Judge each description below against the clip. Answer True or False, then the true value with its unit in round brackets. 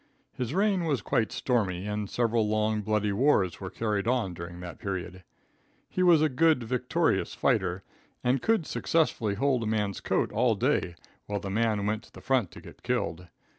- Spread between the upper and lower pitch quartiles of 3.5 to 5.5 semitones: True (4.6 semitones)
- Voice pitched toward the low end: True (110 Hz)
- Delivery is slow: False (180 wpm)